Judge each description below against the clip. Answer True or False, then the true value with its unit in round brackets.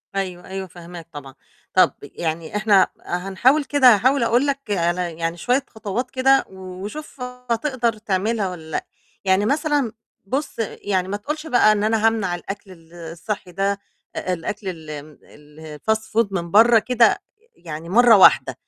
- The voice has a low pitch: False (205 Hz)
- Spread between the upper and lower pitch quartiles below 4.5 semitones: False (5.3 semitones)